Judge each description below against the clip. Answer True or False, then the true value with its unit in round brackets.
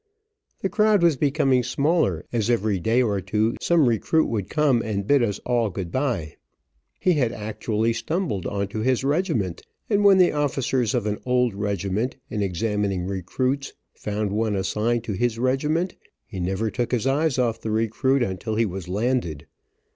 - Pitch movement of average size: True (4.6 semitones)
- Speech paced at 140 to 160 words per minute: False (170 wpm)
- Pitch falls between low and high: False (115 Hz)